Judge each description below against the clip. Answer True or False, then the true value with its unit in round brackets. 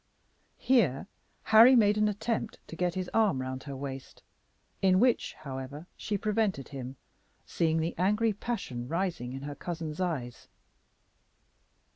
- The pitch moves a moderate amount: False (7.6 semitones)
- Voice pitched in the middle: True (175 Hz)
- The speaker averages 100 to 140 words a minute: True (135 wpm)